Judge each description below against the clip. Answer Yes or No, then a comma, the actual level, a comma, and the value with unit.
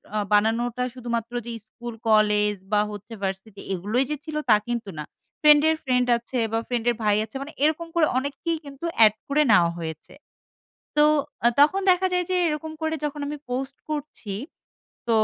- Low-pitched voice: No, high, 245 Hz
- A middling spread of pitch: No, wide, 5.8 semitones